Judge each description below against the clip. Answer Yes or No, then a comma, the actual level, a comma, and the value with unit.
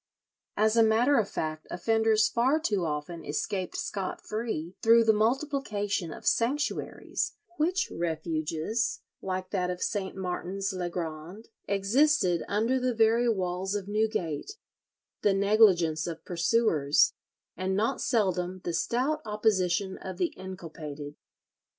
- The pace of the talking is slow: Yes, slow, 120 wpm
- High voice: Yes, high, 195 Hz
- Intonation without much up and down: No, average, 4.4 semitones